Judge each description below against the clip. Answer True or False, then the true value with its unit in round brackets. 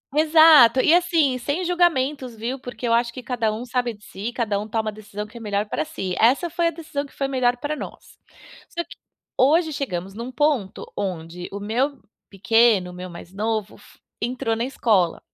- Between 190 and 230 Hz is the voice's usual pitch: False (240 Hz)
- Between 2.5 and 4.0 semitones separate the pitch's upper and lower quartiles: False (5.2 semitones)